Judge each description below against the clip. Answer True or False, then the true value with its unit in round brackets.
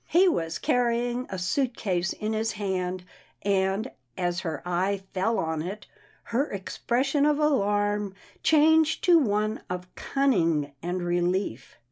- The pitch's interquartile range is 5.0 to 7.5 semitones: True (5.5 semitones)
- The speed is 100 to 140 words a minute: True (135 wpm)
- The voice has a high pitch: True (205 Hz)